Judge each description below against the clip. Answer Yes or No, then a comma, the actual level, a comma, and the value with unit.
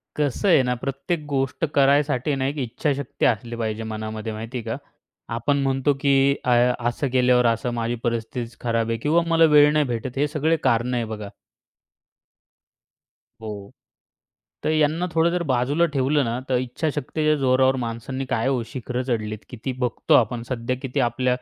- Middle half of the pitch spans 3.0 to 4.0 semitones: Yes, average, 3.4 semitones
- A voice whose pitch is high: No, low, 130 Hz